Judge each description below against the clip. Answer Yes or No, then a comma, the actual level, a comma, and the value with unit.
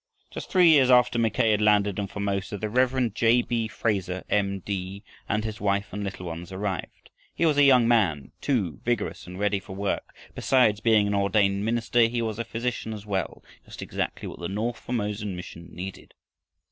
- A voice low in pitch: Yes, low, 105 Hz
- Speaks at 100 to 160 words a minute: No, average, 190 wpm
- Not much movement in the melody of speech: No, average, 3.0 semitones